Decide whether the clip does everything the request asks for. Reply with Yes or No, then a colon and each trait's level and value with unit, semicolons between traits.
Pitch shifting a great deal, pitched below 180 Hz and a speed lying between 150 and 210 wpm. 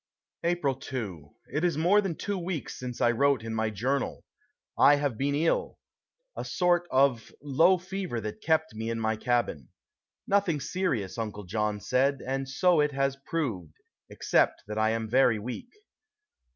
Yes: wide, 6.5 semitones; low, 135 Hz; average, 165 wpm